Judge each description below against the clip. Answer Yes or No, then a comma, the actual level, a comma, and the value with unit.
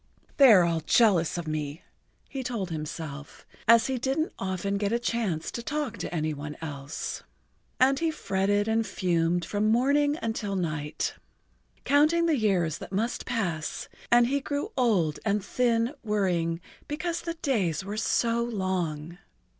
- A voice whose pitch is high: Yes, high, 205 Hz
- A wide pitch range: Yes, wide, 6.5 semitones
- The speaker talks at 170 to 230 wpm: No, average, 155 wpm